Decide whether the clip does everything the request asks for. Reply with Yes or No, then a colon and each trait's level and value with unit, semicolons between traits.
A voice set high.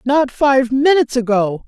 Yes: very high, 260 Hz